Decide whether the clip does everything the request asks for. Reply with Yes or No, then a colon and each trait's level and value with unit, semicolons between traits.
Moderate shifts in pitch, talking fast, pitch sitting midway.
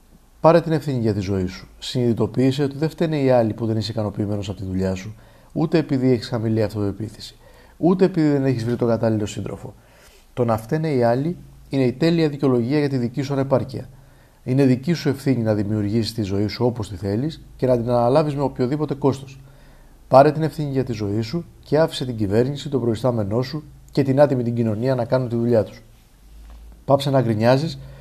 No: average, 4.2 semitones; fast, 200 wpm; low, 130 Hz